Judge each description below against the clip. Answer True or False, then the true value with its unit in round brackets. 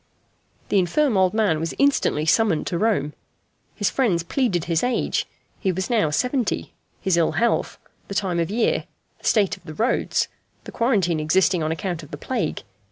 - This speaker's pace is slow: False (175 wpm)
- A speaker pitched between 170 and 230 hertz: True (190 Hz)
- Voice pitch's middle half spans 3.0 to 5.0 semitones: False (5.4 semitones)